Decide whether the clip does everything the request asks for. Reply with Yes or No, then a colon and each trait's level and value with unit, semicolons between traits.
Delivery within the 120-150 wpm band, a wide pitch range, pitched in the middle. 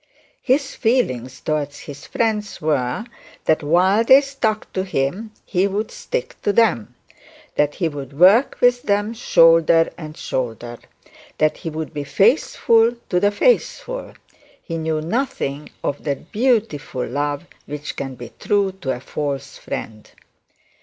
Yes: average, 140 wpm; wide, 7.4 semitones; medium, 165 Hz